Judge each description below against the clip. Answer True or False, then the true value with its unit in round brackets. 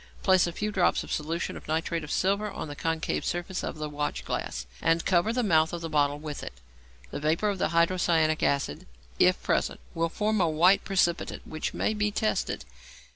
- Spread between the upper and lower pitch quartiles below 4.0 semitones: True (3.4 semitones)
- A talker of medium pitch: True (165 Hz)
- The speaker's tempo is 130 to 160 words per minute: False (195 wpm)